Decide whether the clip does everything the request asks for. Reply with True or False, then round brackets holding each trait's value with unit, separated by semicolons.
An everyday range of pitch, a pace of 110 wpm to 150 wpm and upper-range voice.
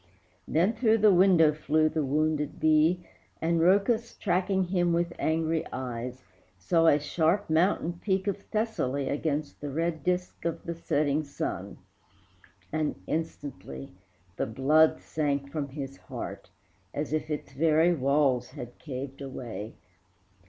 False (3.6 semitones; 135 wpm; 155 Hz)